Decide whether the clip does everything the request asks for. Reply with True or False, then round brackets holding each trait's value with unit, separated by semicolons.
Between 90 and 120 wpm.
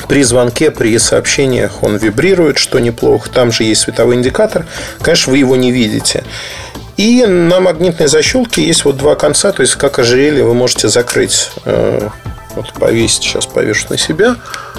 False (160 wpm)